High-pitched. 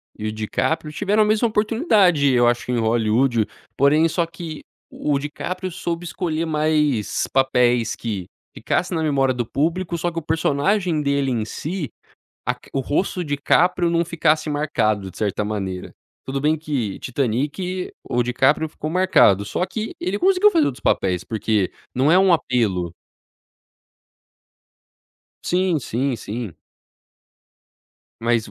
No: medium, 145 Hz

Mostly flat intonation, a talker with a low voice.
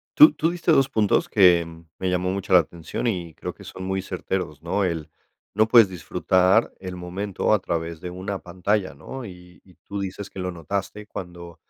Yes: narrow, 2.3 semitones; very low, 95 Hz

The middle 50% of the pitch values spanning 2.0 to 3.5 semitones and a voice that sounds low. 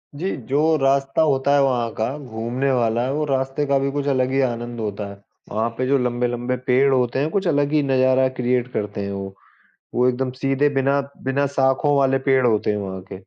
Yes: narrow, 2.4 semitones; low, 130 Hz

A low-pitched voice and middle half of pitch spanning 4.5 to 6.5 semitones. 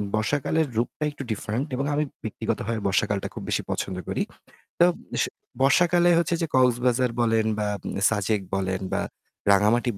Yes: low, 120 Hz; average, 5.2 semitones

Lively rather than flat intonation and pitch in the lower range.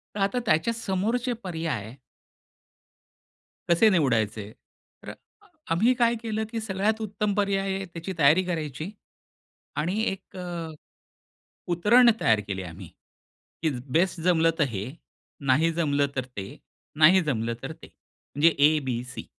No: wide, 5.7 semitones; medium, 170 Hz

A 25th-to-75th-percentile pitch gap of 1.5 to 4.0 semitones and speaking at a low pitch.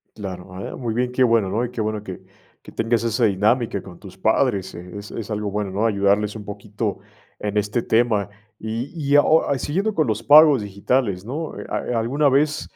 Yes: average, 3.6 semitones; low, 110 Hz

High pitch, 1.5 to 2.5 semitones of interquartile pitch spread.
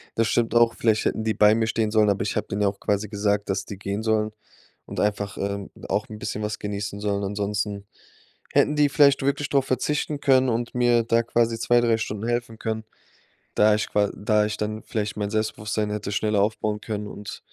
No: low, 105 Hz; narrow, 2.0 semitones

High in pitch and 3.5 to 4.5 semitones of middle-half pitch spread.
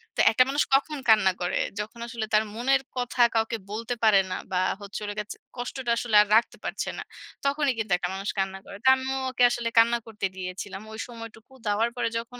No: high, 230 Hz; average, 2.9 semitones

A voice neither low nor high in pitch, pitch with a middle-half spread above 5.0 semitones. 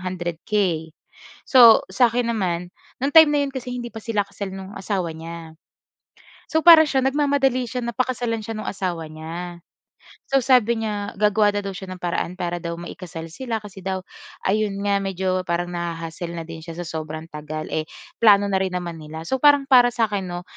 No: high, 195 Hz; wide, 5.4 semitones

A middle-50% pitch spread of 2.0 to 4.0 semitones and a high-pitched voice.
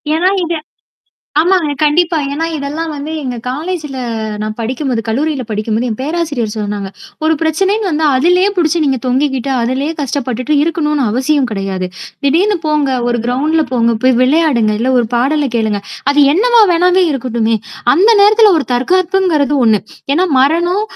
No: average, 5.1 semitones; very high, 290 Hz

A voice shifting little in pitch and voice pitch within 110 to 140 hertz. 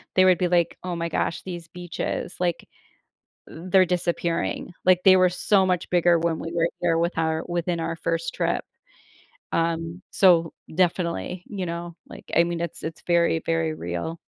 No: narrow, 1.4 semitones; medium, 170 Hz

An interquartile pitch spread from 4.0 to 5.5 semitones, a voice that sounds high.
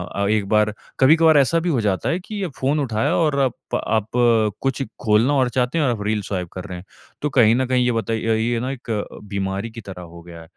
No: average, 4.7 semitones; low, 115 Hz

